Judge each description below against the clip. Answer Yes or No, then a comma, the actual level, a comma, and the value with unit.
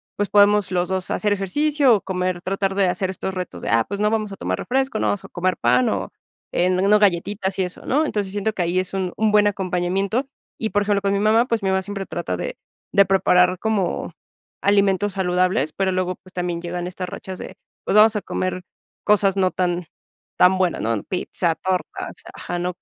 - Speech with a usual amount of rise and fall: No, narrow, 2.3 semitones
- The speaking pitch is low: No, high, 190 Hz